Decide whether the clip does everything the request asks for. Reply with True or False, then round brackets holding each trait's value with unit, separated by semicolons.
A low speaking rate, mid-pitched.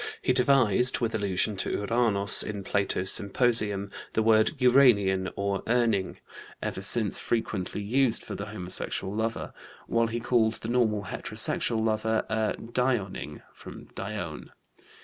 False (130 wpm; 110 Hz)